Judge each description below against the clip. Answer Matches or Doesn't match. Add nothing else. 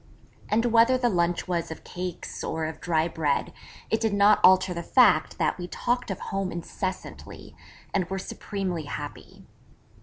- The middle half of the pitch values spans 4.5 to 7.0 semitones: Doesn't match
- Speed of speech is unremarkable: Matches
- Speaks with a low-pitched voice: Doesn't match